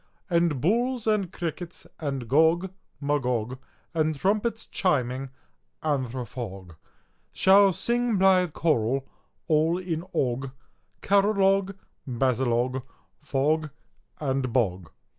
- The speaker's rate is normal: No, slow, 90 wpm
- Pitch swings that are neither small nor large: No, wide, 6.6 semitones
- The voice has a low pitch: No, medium, 155 Hz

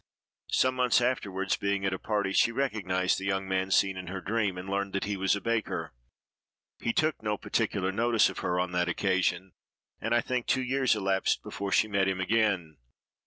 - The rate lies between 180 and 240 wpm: Yes, average, 200 wpm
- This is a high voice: No, low, 100 Hz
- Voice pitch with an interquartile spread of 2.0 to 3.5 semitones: Yes, average, 3.2 semitones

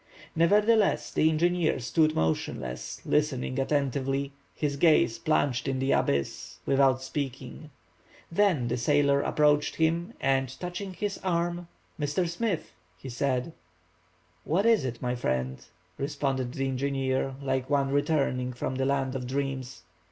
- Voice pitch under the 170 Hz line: Yes, medium, 140 Hz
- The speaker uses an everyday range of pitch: Yes, average, 3.5 semitones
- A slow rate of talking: Yes, slow, 130 wpm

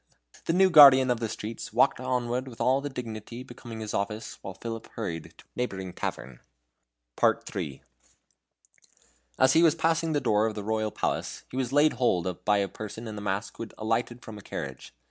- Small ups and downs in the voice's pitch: No, average, 3.7 semitones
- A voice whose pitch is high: No, low, 115 Hz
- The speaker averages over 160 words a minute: Yes, average, 200 wpm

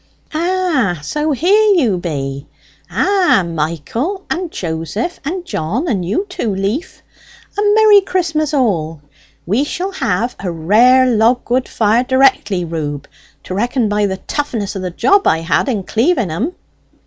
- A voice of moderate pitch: No, high, 235 Hz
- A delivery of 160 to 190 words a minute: No, average, 150 wpm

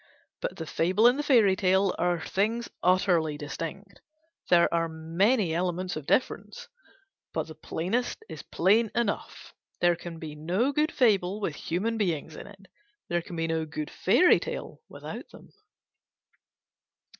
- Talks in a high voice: No, medium, 180 Hz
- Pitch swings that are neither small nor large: Yes, average, 4.3 semitones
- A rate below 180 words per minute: Yes, average, 150 wpm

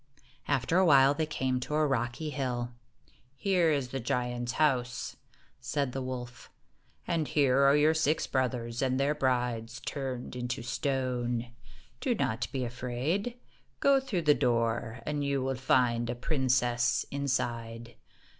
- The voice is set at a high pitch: No, low, 130 Hz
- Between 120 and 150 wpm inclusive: Yes, average, 145 wpm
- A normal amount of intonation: Yes, average, 3.1 semitones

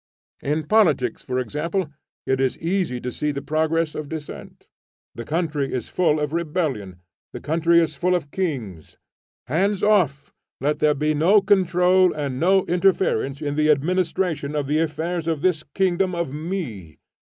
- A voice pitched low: No, medium, 155 Hz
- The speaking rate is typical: Yes, average, 160 wpm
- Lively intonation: No, average, 4.0 semitones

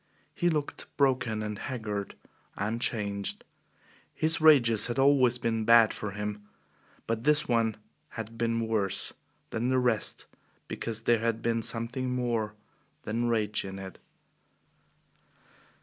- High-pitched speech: No, low, 115 Hz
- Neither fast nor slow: No, slow, 130 wpm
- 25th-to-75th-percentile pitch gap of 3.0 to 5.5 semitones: No, narrow, 2.5 semitones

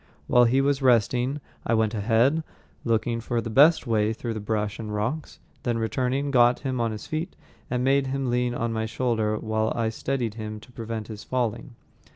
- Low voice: Yes, low, 115 Hz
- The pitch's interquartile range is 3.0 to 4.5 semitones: No, narrow, 2.6 semitones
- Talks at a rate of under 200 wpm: Yes, average, 190 wpm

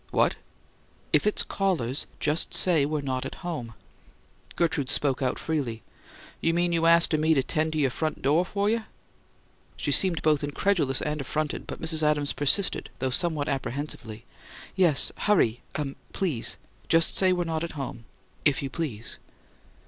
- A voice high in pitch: No, medium, 155 Hz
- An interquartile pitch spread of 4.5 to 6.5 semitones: No, average, 3.7 semitones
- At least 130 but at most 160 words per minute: Yes, average, 155 wpm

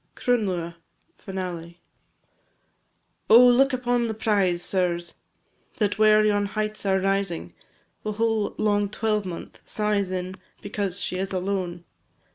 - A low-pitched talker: No, high, 200 Hz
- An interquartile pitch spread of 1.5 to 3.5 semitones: Yes, average, 2.7 semitones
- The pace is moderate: No, slow, 115 wpm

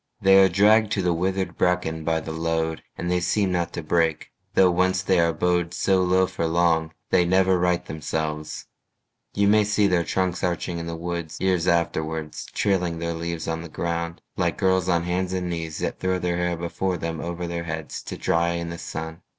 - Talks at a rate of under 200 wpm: No, fast, 205 wpm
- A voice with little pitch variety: Yes, narrow, 2.0 semitones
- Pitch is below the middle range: Yes, very low, 85 Hz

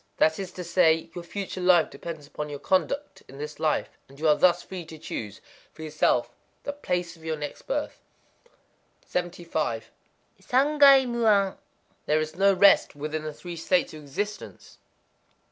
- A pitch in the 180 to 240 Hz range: No, medium, 170 Hz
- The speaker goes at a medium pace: Yes, average, 160 wpm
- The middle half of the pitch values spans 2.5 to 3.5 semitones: No, average, 4.1 semitones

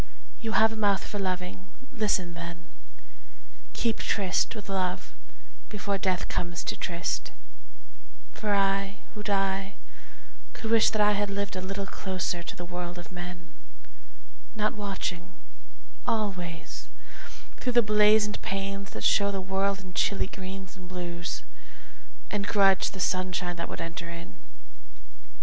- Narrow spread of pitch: Yes, narrow, 2.3 semitones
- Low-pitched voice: No, high, 195 Hz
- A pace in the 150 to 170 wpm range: No, average, 140 wpm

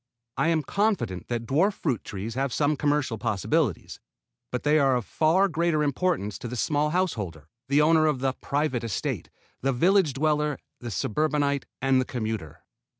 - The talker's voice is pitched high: No, medium, 140 Hz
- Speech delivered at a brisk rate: No, average, 165 wpm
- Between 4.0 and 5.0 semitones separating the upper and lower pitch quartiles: Yes, average, 4.6 semitones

